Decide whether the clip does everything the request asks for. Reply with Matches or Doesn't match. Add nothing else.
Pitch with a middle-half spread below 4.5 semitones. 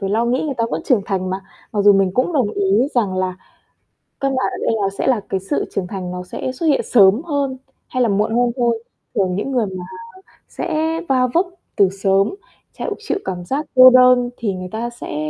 Doesn't match